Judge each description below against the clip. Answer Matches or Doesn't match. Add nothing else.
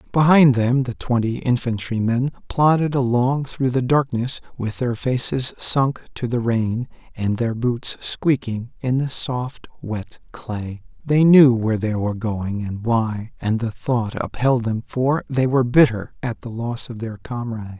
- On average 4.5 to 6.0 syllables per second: Doesn't match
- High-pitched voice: Doesn't match